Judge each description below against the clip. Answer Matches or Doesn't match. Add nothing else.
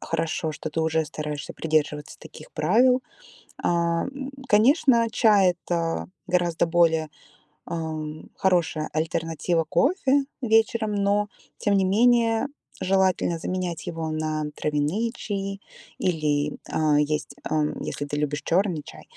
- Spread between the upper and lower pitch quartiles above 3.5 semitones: Matches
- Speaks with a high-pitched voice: Doesn't match